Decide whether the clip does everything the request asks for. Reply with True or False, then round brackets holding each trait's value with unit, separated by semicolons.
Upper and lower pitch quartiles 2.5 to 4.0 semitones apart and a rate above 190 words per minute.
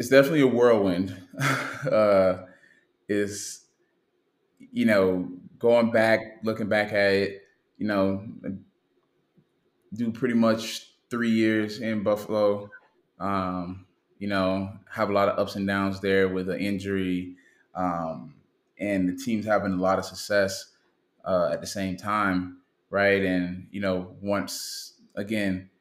False (2.8 semitones; 135 wpm)